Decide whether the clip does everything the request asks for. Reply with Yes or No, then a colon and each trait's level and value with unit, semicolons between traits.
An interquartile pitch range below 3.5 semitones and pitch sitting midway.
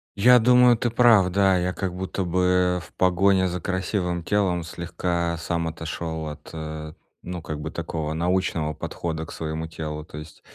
No: average, 2.7 semitones; very low, 90 Hz